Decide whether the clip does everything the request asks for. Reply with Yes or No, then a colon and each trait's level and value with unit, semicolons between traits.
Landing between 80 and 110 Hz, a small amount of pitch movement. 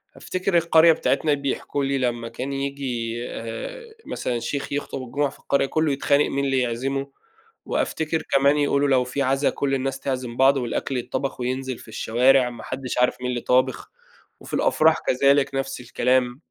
No: low, 135 Hz; narrow, 2.0 semitones